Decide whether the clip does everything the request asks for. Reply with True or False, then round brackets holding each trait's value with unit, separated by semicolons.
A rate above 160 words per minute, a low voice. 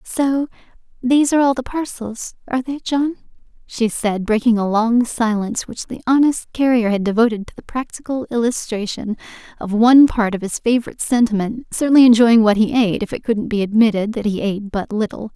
False (180 wpm; 230 Hz)